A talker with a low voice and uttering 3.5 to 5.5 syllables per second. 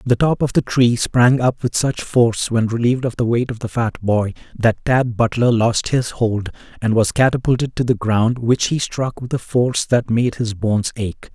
Yes: low, 120 Hz; 4.8 syllables/s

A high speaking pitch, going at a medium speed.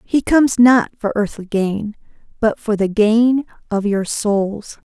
Yes: high, 215 Hz; average, 160 wpm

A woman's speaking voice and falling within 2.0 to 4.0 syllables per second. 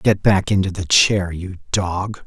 No: male; 3.9 syllables/s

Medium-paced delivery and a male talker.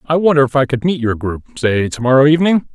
No: fast, 240 wpm; male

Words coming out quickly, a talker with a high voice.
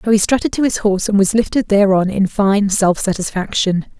Yes: fast, 210 wpm; high, 205 Hz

